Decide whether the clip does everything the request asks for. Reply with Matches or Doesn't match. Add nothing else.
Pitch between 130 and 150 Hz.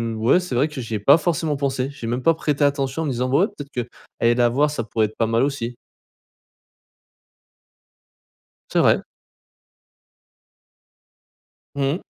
Matches